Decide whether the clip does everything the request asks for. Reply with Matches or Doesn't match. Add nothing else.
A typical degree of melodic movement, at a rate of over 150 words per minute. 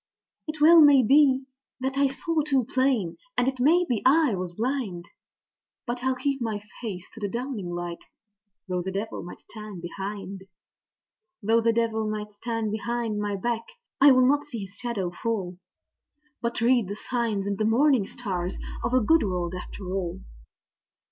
Matches